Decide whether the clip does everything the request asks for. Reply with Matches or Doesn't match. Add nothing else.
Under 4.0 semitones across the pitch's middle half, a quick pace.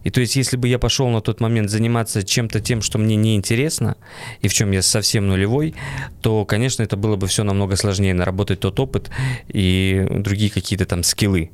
Matches